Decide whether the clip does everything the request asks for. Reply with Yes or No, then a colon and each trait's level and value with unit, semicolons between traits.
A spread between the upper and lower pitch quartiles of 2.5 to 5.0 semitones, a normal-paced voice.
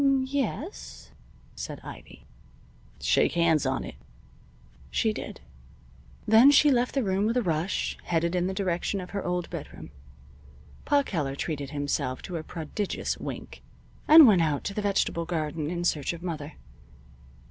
No: wide, 5.5 semitones; average, 160 wpm